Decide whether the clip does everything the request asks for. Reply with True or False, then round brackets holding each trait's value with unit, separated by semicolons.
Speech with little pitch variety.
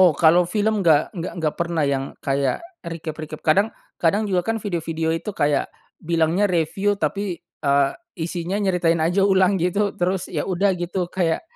False (3.1 semitones)